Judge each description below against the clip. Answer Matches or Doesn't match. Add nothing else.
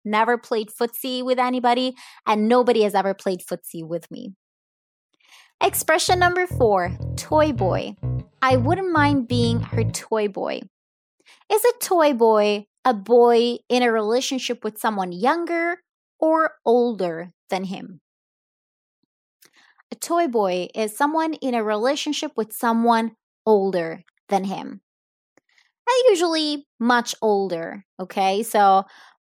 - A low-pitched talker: Doesn't match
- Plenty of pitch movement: Matches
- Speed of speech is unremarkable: Doesn't match